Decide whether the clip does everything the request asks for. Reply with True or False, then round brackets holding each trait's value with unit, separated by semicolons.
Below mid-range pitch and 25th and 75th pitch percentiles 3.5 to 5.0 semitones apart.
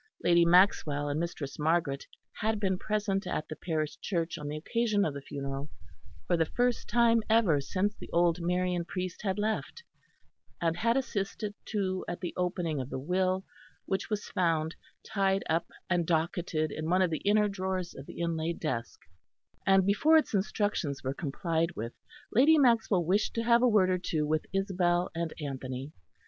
False (180 Hz; 4.3 semitones)